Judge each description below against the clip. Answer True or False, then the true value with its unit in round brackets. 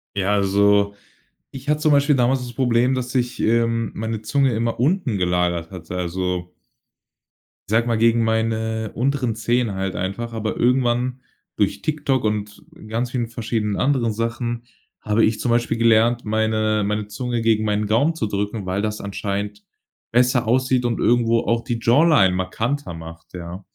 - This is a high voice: False (115 Hz)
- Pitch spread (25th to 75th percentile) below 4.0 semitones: True (2.9 semitones)